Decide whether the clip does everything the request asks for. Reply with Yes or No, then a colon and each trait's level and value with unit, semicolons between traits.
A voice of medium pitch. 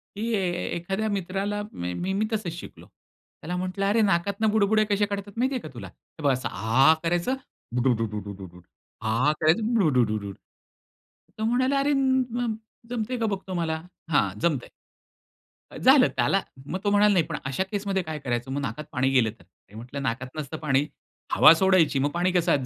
Yes: medium, 170 Hz